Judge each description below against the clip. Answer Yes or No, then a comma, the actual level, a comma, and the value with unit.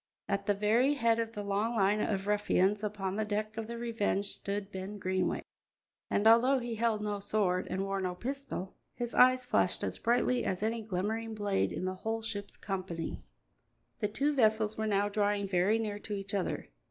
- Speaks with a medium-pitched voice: No, high, 210 Hz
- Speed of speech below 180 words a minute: No, average, 190 wpm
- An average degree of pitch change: No, narrow, 2.3 semitones